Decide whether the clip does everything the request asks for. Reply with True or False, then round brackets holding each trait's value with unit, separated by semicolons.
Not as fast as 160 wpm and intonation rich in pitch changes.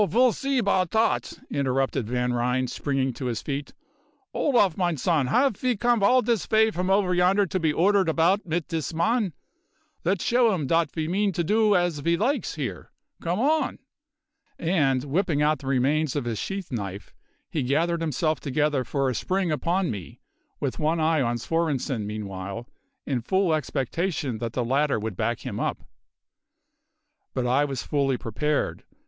False (170 wpm; 6.4 semitones)